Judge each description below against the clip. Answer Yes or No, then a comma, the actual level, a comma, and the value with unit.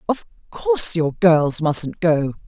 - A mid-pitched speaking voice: Yes, medium, 175 Hz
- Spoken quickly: No, average, 145 wpm